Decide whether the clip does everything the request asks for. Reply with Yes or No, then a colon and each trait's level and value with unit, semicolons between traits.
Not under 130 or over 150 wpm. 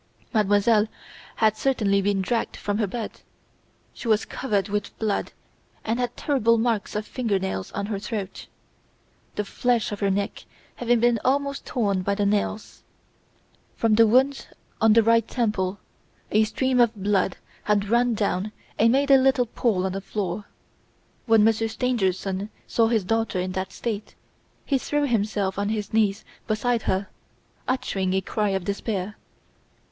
No: average, 160 wpm